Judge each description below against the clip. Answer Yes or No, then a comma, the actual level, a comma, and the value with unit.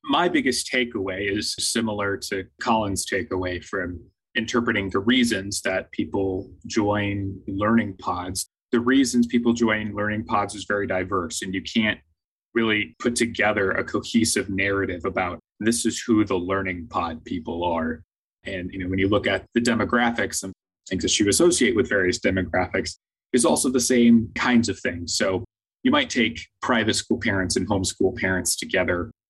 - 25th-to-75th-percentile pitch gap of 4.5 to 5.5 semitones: No, average, 3.4 semitones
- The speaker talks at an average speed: Yes, average, 160 wpm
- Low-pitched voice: Yes, low, 105 Hz